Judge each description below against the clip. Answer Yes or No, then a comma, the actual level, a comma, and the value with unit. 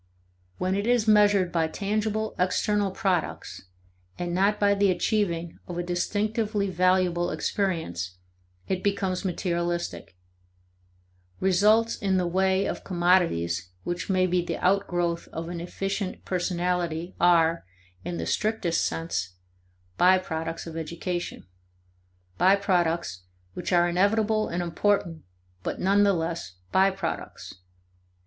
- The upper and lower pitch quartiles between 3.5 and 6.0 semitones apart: No, average, 2.7 semitones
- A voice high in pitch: No, medium, 180 Hz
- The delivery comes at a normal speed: No, slow, 120 wpm